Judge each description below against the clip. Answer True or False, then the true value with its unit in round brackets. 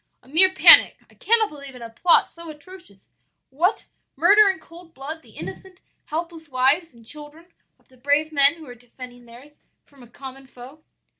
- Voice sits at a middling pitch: False (295 Hz)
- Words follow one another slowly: False (180 wpm)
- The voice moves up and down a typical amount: True (4.6 semitones)